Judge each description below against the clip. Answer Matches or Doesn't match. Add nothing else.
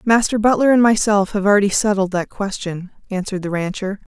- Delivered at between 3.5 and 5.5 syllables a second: Doesn't match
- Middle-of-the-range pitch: Doesn't match